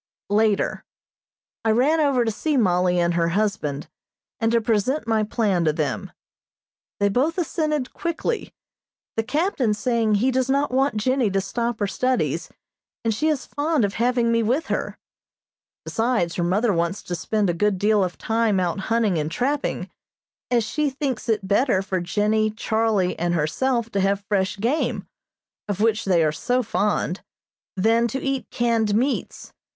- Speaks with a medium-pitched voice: No, high, 220 Hz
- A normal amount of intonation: Yes, average, 4.5 semitones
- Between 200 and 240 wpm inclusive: No, average, 165 wpm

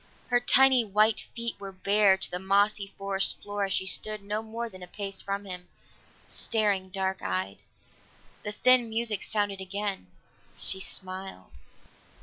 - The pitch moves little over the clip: Yes, narrow, 2.1 semitones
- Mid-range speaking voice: No, high, 200 Hz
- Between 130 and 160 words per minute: Yes, average, 150 wpm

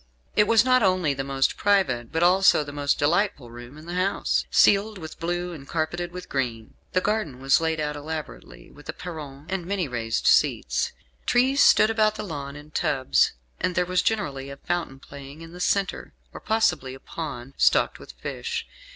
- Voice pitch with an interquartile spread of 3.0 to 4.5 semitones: No, average, 5.1 semitones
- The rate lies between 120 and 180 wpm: No, average, 190 wpm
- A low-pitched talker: No, medium, 160 Hz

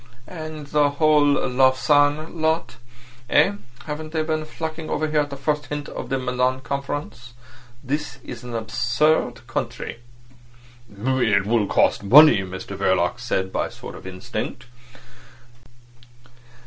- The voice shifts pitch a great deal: No, average, 4.1 semitones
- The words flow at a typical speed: No, slow, 130 wpm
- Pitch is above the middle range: No, low, 135 Hz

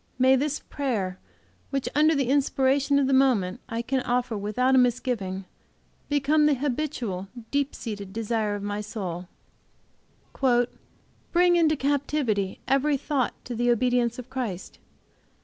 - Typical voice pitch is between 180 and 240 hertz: No, very high, 255 Hz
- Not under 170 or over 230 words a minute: No, slow, 135 wpm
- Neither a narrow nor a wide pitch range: Yes, average, 4.8 semitones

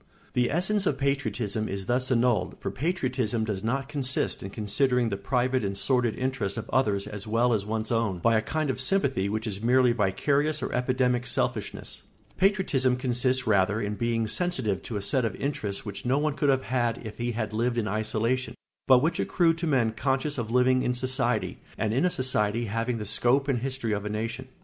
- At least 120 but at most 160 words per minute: No, fast, 205 wpm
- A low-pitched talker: Yes, low, 125 Hz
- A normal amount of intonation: Yes, average, 3.4 semitones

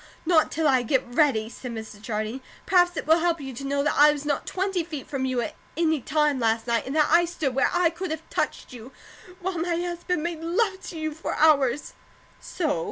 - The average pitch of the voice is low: No, very high, 300 Hz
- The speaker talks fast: Yes, fast, 225 wpm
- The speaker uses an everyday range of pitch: Yes, average, 4.6 semitones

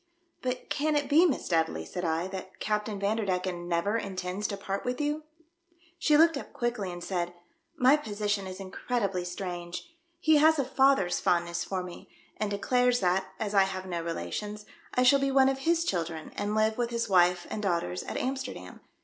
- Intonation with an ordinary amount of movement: No, wide, 6.5 semitones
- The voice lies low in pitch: No, high, 205 Hz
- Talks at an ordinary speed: Yes, average, 195 wpm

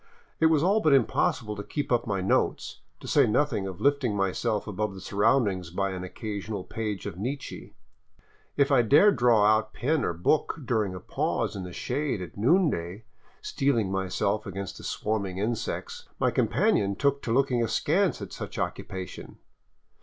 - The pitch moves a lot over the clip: Yes, wide, 5.9 semitones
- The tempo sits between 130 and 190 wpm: Yes, average, 170 wpm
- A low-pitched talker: Yes, low, 110 Hz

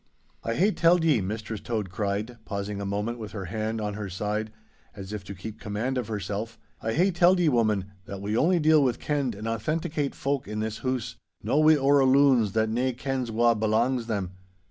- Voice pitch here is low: Yes, low, 115 Hz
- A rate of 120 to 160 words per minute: No, average, 200 wpm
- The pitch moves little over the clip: No, average, 4.3 semitones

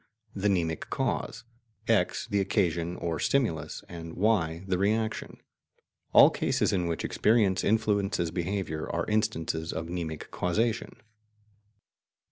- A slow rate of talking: Yes, slow, 115 wpm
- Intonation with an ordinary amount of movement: Yes, average, 4.0 semitones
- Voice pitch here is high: No, very low, 90 Hz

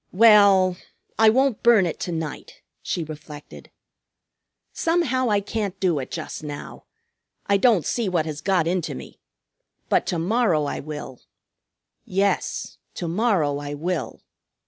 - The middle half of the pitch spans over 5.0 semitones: Yes, wide, 5.5 semitones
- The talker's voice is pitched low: No, medium, 185 Hz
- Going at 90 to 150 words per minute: Yes, average, 140 wpm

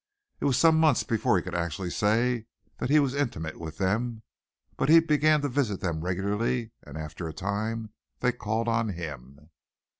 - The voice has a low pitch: Yes, low, 110 Hz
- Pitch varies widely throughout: Yes, wide, 6.1 semitones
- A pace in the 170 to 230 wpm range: Yes, average, 180 wpm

